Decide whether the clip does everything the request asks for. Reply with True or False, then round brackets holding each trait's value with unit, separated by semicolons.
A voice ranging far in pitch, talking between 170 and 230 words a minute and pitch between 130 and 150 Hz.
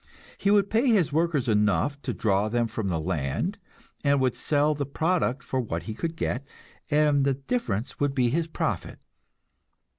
True (5.9 semitones; 175 wpm; 140 Hz)